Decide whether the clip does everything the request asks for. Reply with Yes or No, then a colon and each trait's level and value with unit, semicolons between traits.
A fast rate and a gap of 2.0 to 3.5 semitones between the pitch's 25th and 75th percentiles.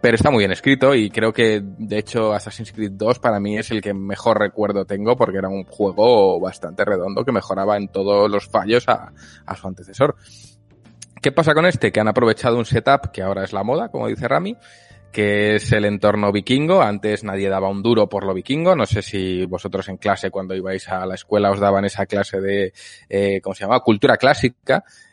Yes: fast, 215 wpm; average, 2.8 semitones